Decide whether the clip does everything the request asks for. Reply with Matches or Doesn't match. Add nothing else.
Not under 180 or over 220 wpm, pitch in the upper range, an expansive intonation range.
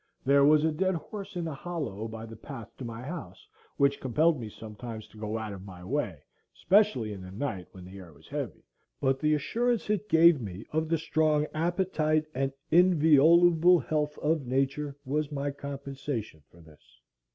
Doesn't match